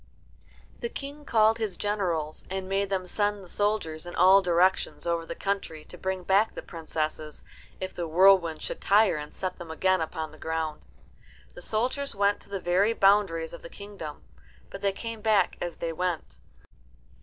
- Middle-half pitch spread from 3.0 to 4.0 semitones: Yes, average, 3.6 semitones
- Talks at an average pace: Yes, average, 180 wpm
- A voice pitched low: No, medium, 185 Hz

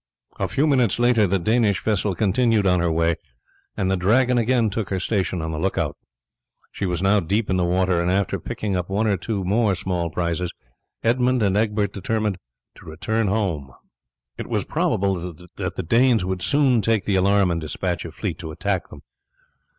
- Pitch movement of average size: Yes, average, 3.7 semitones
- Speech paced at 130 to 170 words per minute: No, average, 195 wpm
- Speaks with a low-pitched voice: Yes, low, 100 Hz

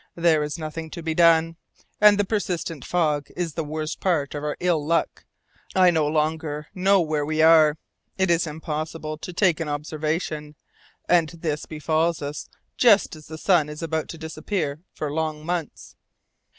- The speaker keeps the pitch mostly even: Yes, narrow, 1.9 semitones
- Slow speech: No, average, 170 wpm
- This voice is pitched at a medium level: Yes, medium, 160 Hz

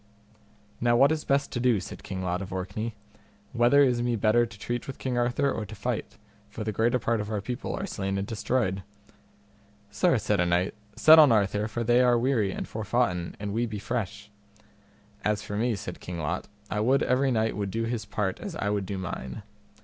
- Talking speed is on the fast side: Yes, fast, 210 wpm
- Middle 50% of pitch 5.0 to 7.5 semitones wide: No, average, 3.4 semitones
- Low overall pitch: Yes, low, 110 Hz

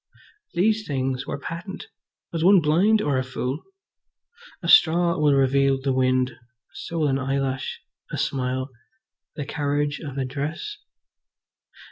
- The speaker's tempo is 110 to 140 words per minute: Yes, slow, 135 wpm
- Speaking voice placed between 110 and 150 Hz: Yes, medium, 140 Hz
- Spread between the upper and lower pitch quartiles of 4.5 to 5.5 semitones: No, average, 4.0 semitones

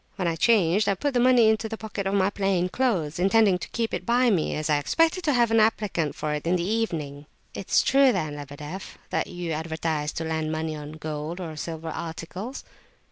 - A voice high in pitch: No, medium, 180 Hz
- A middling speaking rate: No, fast, 215 wpm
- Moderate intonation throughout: No, wide, 5.9 semitones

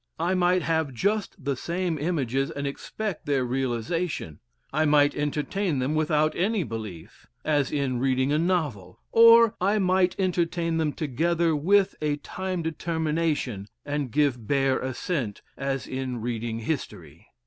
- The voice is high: No, medium, 150 Hz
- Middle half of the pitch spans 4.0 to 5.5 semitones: Yes, average, 4.8 semitones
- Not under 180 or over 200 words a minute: No, average, 140 wpm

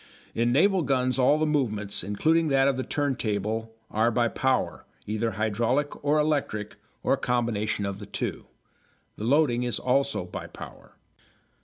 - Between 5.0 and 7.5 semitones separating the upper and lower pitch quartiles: No, average, 4.6 semitones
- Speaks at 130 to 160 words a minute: Yes, average, 155 wpm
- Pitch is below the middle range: Yes, low, 125 Hz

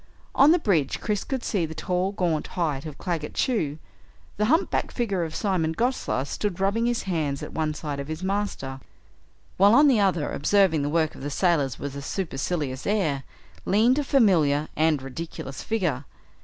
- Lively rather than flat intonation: Yes, wide, 5.8 semitones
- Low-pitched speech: No, medium, 170 Hz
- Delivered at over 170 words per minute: Yes, average, 180 wpm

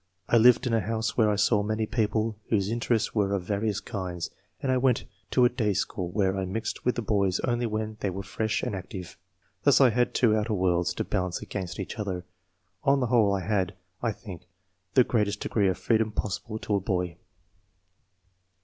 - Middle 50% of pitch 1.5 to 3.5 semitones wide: Yes, average, 3.1 semitones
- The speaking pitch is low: Yes, low, 105 Hz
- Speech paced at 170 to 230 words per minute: Yes, fast, 205 wpm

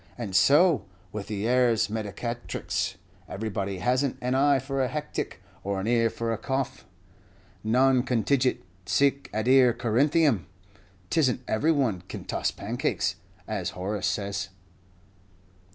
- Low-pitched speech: Yes, low, 120 Hz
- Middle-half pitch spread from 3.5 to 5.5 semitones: Yes, average, 4.4 semitones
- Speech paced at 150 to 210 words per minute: No, slow, 135 wpm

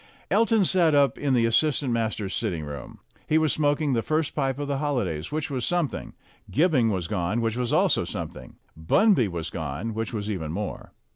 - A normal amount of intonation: No, wide, 6.9 semitones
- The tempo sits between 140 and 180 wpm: No, average, 190 wpm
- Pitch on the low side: Yes, low, 120 Hz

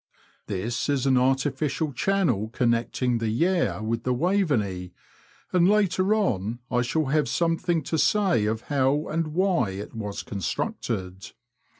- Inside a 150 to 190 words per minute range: No, slow, 135 wpm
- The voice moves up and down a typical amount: No, wide, 6.7 semitones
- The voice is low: Yes, low, 130 Hz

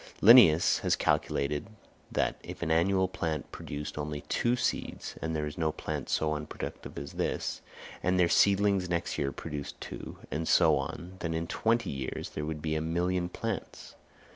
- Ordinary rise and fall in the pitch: Yes, average, 3.3 semitones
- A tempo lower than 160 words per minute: No, average, 165 wpm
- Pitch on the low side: Yes, very low, 80 Hz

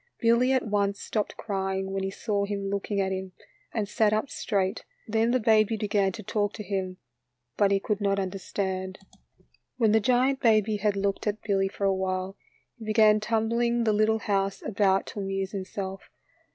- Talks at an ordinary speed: Yes, average, 180 wpm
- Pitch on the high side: Yes, high, 205 Hz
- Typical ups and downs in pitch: No, narrow, 2.1 semitones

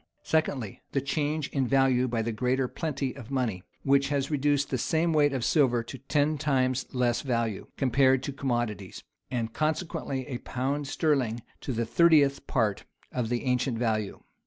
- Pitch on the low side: Yes, low, 130 Hz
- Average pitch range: Yes, average, 3.1 semitones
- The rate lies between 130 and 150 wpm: No, average, 165 wpm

